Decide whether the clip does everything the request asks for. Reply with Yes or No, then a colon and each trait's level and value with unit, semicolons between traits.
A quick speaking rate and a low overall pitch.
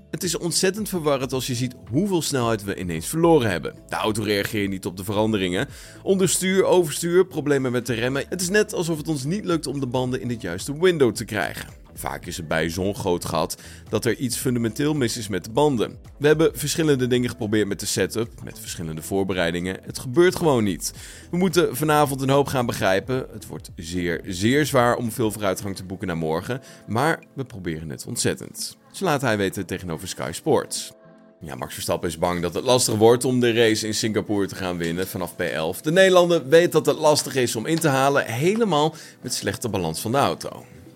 Yes: fast, 210 wpm; low, 120 Hz